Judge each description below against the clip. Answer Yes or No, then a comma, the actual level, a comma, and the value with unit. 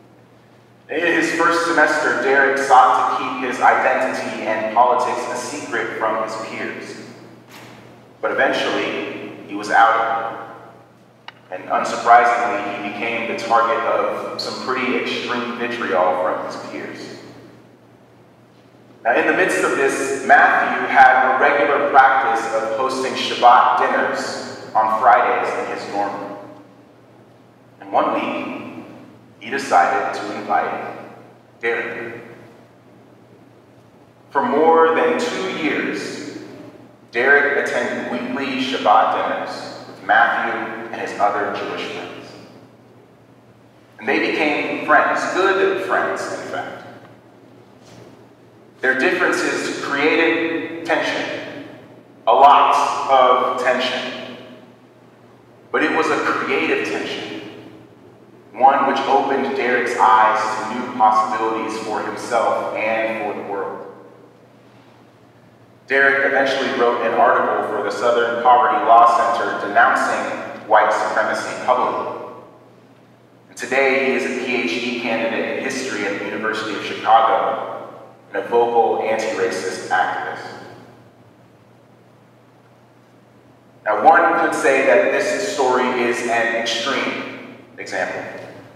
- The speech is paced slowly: Yes, slow, 110 wpm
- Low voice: Yes, low, 120 Hz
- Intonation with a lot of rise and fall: No, average, 3.3 semitones